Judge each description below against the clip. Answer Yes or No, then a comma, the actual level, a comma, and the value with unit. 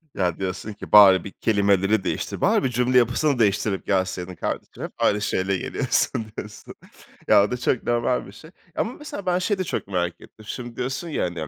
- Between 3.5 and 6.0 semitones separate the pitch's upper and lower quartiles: Yes, average, 4.7 semitones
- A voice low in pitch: Yes, low, 105 Hz